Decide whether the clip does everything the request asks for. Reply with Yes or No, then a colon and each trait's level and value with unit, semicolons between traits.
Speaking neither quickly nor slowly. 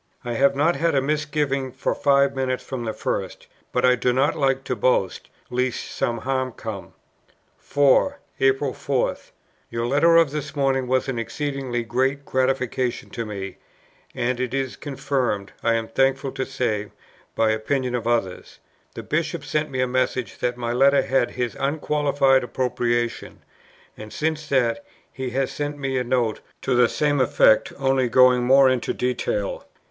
Yes: average, 165 wpm